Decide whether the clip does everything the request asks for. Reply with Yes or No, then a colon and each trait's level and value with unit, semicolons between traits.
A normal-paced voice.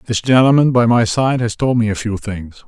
No: fast, 245 wpm